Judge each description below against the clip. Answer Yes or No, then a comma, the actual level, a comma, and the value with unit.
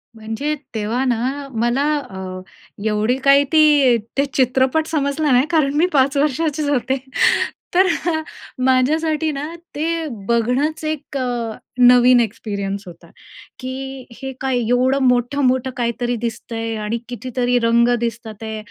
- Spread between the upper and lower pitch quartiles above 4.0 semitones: No, average, 3.4 semitones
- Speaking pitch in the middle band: No, very high, 255 Hz